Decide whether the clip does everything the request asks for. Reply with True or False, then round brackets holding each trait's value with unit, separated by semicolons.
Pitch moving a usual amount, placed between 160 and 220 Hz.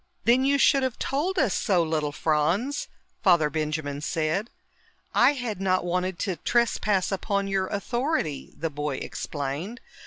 False (7.4 semitones; 190 Hz)